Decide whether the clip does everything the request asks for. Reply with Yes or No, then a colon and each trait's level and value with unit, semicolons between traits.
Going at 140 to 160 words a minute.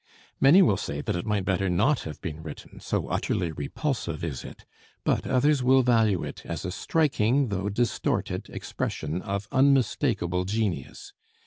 Yes: average, 155 wpm